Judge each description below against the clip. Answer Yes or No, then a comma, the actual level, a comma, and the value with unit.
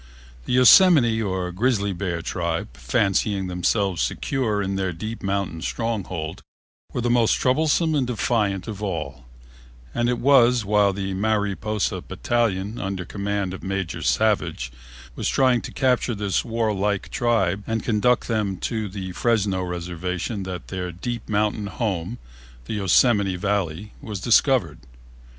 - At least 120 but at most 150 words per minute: Yes, slow, 135 wpm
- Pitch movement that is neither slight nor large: Yes, average, 3.8 semitones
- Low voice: Yes, low, 100 Hz